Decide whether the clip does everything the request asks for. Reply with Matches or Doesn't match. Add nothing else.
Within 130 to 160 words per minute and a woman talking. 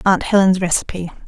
Matches